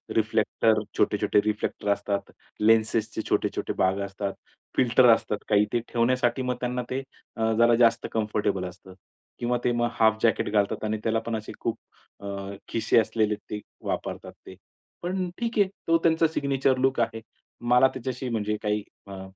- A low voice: Yes, low, 115 Hz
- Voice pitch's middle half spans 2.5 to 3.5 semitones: Yes, average, 2.8 semitones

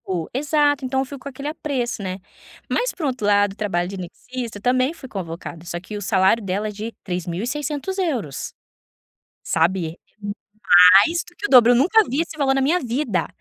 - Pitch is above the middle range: Yes, high, 240 Hz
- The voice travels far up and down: Yes, wide, 6.8 semitones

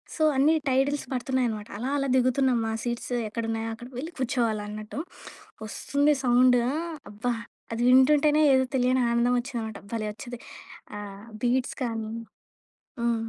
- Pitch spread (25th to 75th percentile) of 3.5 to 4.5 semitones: No, average, 2.7 semitones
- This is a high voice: Yes, high, 245 Hz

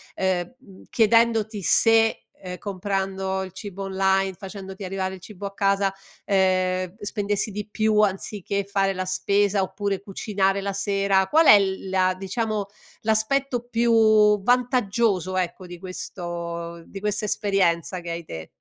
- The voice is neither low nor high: No, high, 195 Hz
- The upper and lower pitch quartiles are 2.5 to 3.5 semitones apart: No, narrow, 2.0 semitones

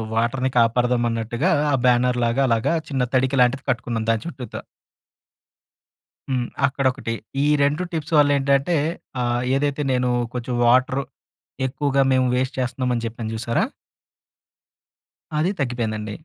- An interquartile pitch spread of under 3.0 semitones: Yes, narrow, 2.5 semitones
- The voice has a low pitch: Yes, low, 125 Hz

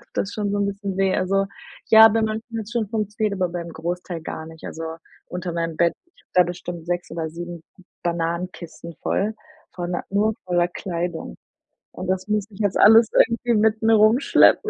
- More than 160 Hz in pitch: Yes, medium, 185 Hz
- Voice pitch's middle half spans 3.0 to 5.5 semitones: Yes, average, 3.7 semitones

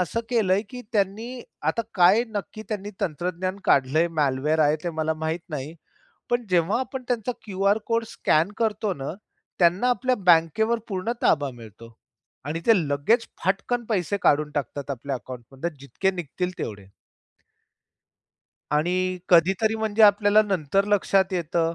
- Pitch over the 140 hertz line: Yes, medium, 185 Hz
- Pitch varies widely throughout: Yes, wide, 5.7 semitones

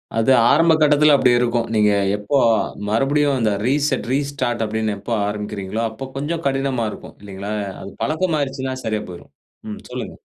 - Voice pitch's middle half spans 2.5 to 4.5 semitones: No, average, 4.9 semitones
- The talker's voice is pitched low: Yes, low, 130 Hz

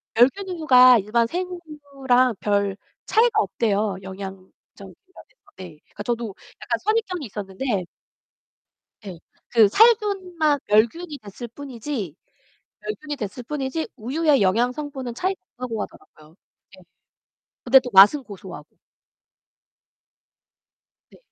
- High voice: Yes, very high, 250 Hz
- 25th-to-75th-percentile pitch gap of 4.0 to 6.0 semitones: No, wide, 6.8 semitones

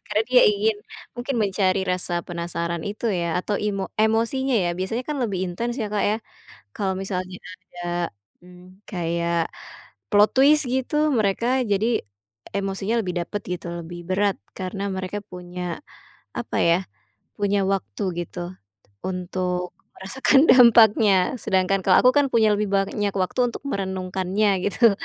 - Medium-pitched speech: No, high, 195 Hz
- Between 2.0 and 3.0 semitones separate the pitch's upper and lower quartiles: No, average, 3.5 semitones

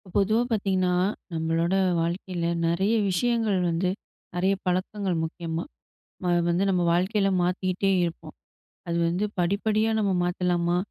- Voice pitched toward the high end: No, medium, 180 Hz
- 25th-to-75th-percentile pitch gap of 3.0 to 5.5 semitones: No, narrow, 2.4 semitones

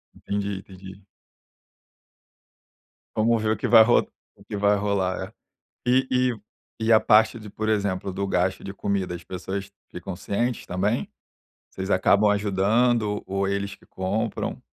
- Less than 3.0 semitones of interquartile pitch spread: Yes, narrow, 2.4 semitones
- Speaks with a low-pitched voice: Yes, low, 100 Hz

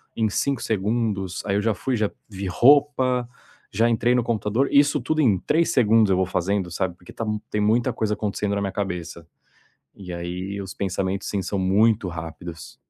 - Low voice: Yes, low, 105 Hz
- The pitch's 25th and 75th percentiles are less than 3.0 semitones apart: No, average, 3.7 semitones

